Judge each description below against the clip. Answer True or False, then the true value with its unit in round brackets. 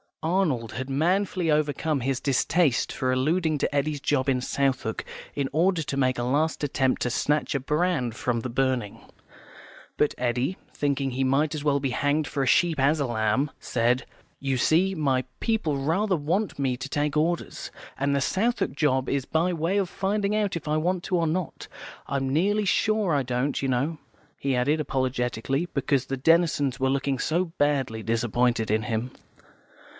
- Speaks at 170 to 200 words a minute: True (180 wpm)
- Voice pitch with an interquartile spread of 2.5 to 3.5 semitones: False (4.0 semitones)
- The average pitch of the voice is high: False (140 Hz)